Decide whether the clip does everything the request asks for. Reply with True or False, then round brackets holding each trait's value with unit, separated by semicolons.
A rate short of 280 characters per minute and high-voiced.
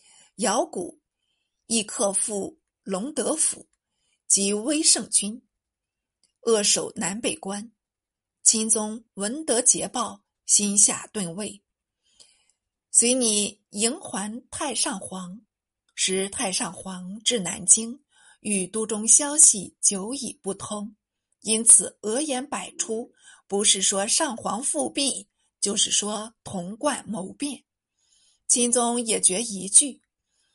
True (150 characters per minute; 220 Hz)